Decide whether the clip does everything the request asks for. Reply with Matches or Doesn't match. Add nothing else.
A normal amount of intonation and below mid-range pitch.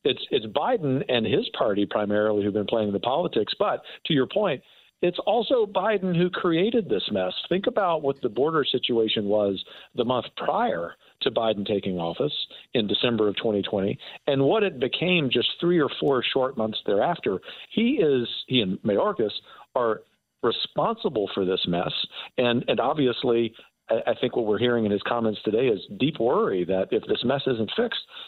Matches